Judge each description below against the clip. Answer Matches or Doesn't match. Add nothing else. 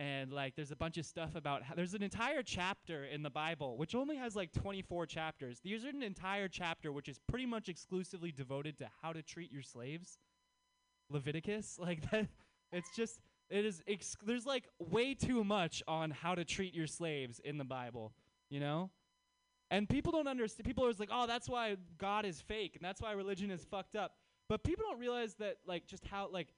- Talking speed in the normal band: Doesn't match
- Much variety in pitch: Matches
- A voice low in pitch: Doesn't match